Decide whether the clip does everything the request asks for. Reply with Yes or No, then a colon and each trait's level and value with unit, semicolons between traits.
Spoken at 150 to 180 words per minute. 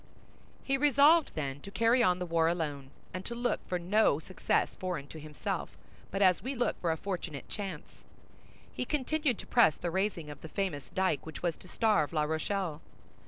No: average, 190 wpm